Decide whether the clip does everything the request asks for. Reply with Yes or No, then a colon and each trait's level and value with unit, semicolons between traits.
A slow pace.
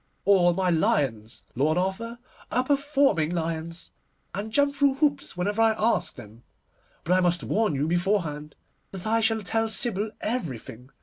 No: average, 150 wpm